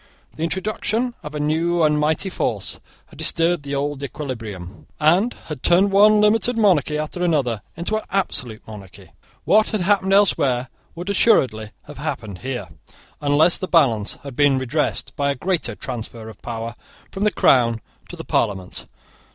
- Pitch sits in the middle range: Yes, medium, 150 Hz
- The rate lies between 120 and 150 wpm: No, average, 160 wpm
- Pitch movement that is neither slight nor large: No, wide, 7.5 semitones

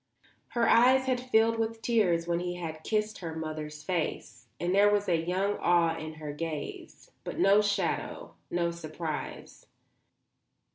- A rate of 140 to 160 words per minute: Yes, average, 145 wpm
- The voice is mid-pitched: Yes, medium, 175 Hz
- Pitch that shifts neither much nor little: Yes, average, 4.6 semitones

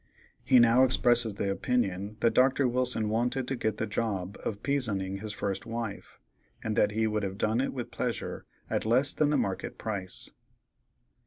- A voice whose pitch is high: No, low, 110 Hz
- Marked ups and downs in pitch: No, average, 3.5 semitones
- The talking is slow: No, average, 175 wpm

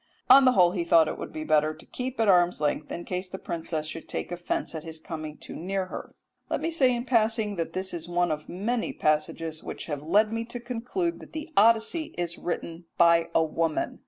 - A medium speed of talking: No, fast, 225 wpm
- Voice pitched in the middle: Yes, medium, 175 Hz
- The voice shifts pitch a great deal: Yes, wide, 5.9 semitones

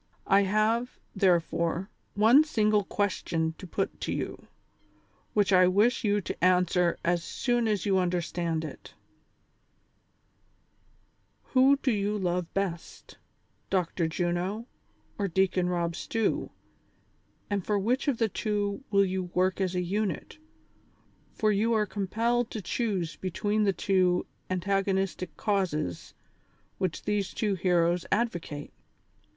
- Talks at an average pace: No, slow, 130 wpm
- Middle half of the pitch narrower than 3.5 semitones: Yes, average, 3.0 semitones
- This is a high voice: Yes, high, 195 Hz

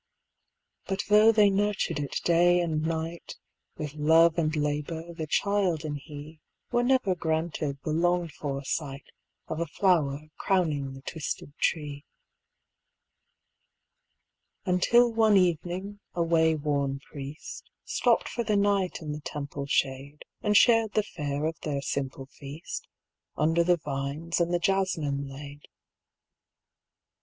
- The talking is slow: Yes, slow, 130 wpm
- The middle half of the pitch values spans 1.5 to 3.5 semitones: No, average, 3.9 semitones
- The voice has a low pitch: No, medium, 160 Hz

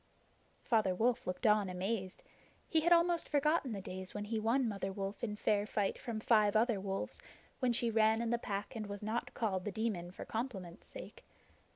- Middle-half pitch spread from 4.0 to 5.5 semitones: No, average, 3.1 semitones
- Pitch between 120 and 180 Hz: No, high, 215 Hz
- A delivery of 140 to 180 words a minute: No, average, 195 wpm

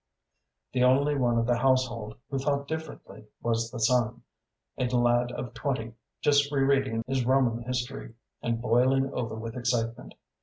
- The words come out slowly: No, average, 155 wpm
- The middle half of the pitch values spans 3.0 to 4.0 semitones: No, narrow, 2.4 semitones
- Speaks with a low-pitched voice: Yes, low, 125 Hz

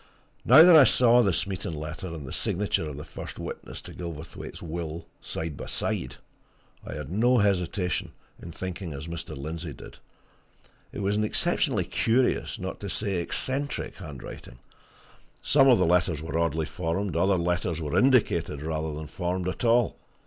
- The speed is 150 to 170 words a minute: Yes, average, 165 wpm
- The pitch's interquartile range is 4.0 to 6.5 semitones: Yes, average, 4.4 semitones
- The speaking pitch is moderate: No, very low, 85 Hz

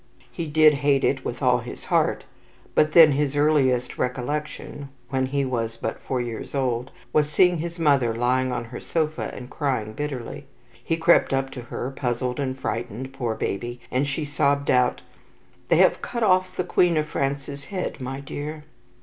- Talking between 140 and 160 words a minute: No, average, 175 wpm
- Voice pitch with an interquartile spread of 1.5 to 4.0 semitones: Yes, average, 3.3 semitones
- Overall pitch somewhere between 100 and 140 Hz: Yes, low, 135 Hz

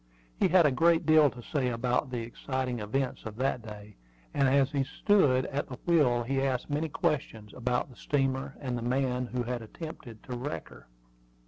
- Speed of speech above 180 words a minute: Yes, average, 195 wpm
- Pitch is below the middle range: Yes, low, 130 Hz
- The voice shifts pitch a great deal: No, average, 2.7 semitones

